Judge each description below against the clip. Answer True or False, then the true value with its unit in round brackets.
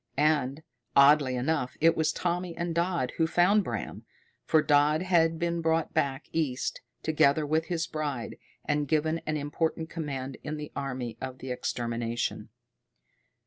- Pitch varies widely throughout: False (3.2 semitones)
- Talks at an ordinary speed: True (145 wpm)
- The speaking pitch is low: False (155 Hz)